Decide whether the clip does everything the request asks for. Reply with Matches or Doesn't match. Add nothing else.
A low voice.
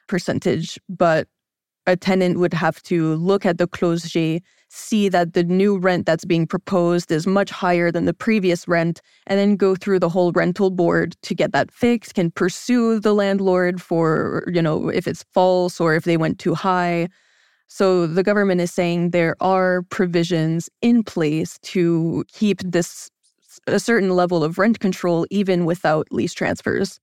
Doesn't match